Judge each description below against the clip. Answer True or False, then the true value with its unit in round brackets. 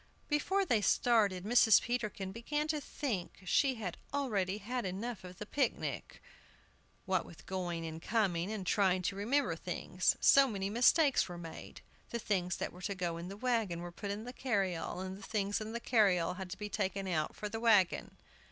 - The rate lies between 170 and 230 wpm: True (190 wpm)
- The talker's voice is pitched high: True (205 Hz)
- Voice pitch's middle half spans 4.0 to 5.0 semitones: True (4.3 semitones)